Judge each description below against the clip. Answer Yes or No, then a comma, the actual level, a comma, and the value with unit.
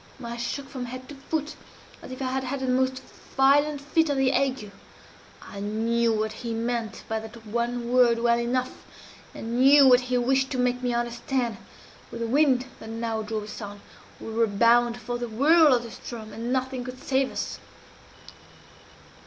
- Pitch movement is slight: Yes, narrow, 2.2 semitones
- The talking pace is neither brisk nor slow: Yes, average, 185 wpm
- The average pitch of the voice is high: Yes, high, 245 Hz